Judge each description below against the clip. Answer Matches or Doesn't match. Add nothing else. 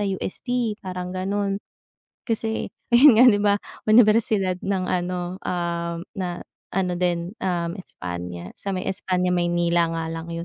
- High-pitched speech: Doesn't match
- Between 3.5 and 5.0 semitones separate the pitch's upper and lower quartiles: Doesn't match